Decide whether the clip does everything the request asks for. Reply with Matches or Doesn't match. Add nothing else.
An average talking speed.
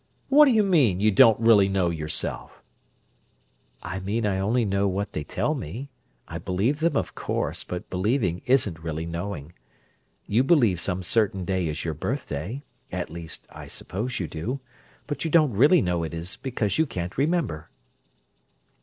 Matches